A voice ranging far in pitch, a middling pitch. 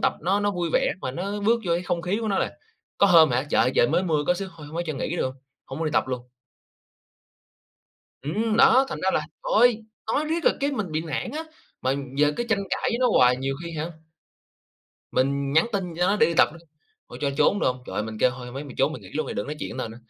Yes: wide, 6.8 semitones; medium, 165 Hz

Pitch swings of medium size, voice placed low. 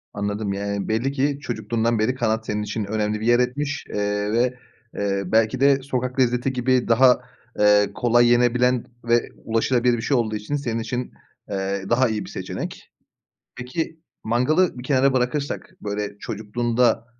Yes: average, 3.1 semitones; low, 120 Hz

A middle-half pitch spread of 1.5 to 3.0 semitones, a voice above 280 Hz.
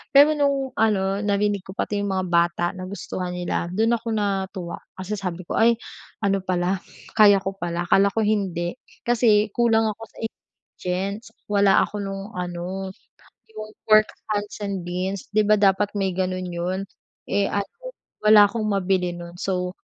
No: narrow, 2.5 semitones; high, 195 Hz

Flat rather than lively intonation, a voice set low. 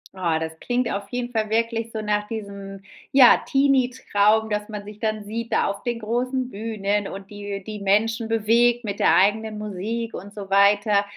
No: narrow, 2.3 semitones; high, 215 Hz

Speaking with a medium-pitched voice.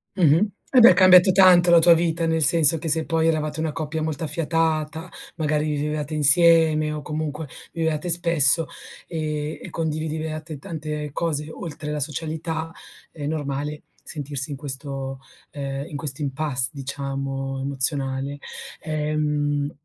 Yes: medium, 155 Hz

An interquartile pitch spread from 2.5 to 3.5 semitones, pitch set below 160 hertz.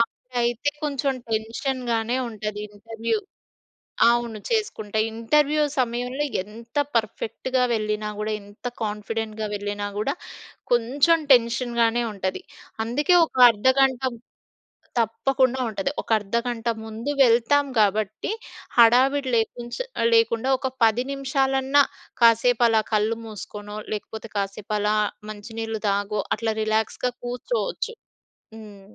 No: average, 3.2 semitones; high, 230 Hz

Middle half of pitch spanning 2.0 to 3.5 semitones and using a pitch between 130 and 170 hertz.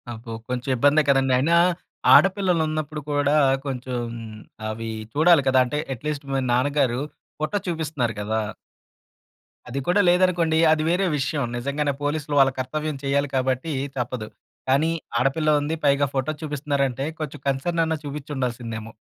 Yes: average, 3.2 semitones; medium, 140 Hz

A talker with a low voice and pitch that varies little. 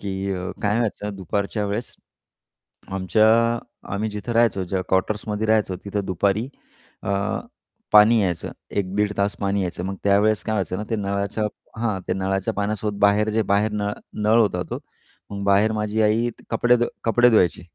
Yes: low, 105 Hz; narrow, 1.8 semitones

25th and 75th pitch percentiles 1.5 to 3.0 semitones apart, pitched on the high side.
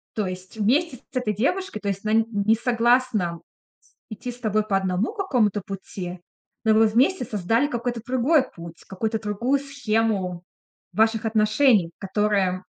No: average, 3.8 semitones; high, 220 Hz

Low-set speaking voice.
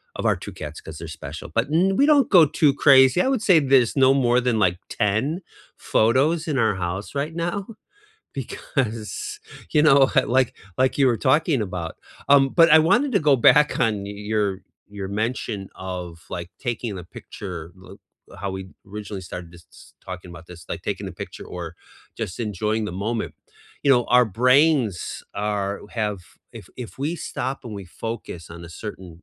Yes: low, 115 Hz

